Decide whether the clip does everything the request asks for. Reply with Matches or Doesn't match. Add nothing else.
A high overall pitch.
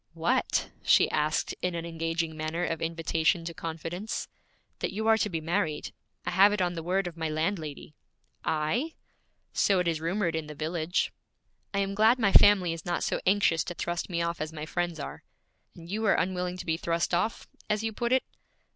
Doesn't match